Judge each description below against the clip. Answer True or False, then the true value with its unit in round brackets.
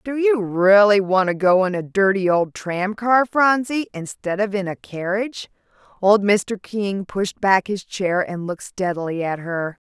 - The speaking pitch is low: False (195 Hz)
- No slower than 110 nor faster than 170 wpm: False (180 wpm)